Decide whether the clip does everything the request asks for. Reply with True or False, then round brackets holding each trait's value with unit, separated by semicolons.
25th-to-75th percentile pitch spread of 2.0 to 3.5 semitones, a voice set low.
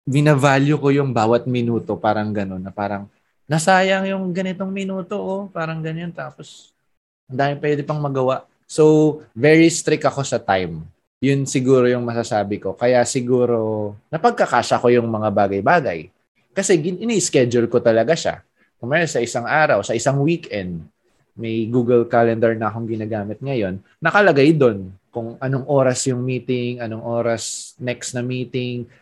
False (4.9 semitones; 125 Hz)